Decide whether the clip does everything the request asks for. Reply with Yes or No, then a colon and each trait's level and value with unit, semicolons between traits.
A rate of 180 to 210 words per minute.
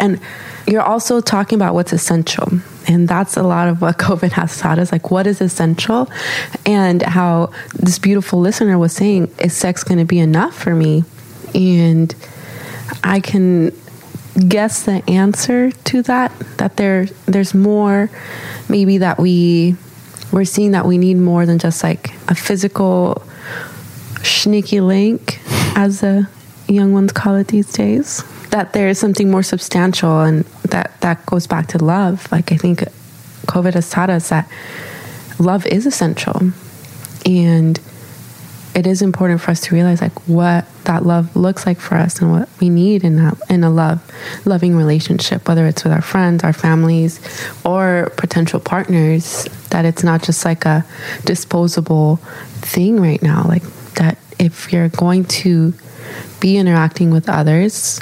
No: average, 160 wpm